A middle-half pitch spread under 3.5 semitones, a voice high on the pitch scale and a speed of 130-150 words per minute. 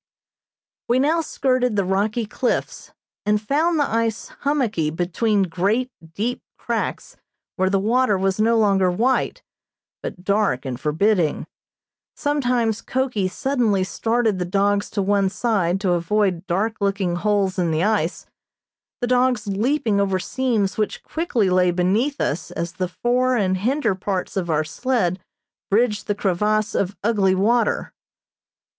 No: average, 4.3 semitones; high, 205 Hz; average, 140 wpm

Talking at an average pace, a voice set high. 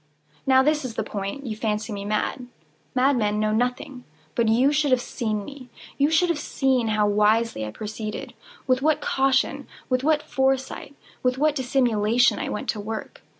Yes: average, 160 wpm; very high, 250 Hz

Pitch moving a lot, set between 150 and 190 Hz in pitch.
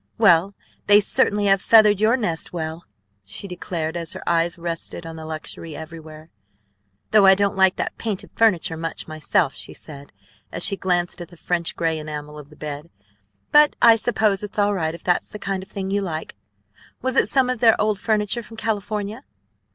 No: average, 4.4 semitones; medium, 185 Hz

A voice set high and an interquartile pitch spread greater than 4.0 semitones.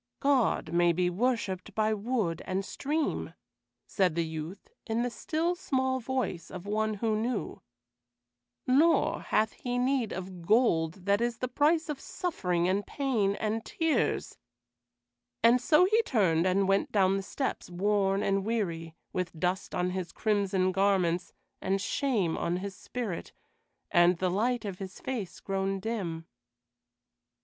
Yes: high, 200 Hz; average, 5.1 semitones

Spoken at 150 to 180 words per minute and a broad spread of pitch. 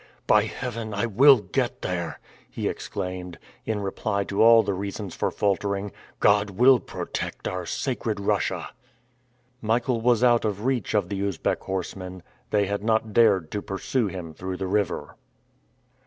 No: average, 155 wpm; average, 2.9 semitones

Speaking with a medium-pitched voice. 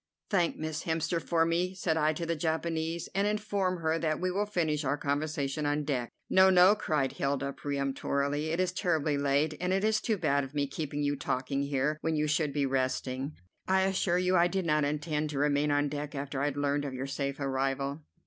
Yes: medium, 150 Hz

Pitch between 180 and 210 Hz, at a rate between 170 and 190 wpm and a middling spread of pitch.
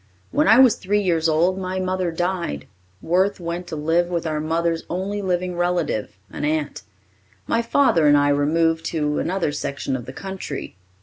No: medium, 170 Hz; average, 175 wpm; average, 3.3 semitones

